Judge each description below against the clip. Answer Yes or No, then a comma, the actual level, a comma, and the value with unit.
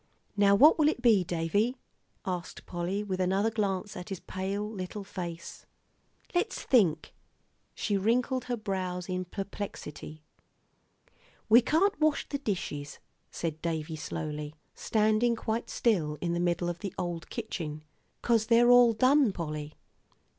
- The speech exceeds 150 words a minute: No, average, 140 wpm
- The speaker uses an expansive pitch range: No, average, 5.0 semitones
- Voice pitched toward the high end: Yes, high, 195 Hz